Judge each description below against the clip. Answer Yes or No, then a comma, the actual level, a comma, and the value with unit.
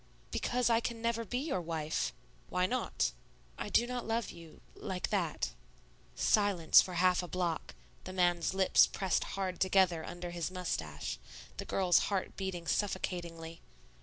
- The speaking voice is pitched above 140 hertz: Yes, medium, 185 Hz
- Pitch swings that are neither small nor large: Yes, average, 3.0 semitones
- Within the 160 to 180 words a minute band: No, average, 150 wpm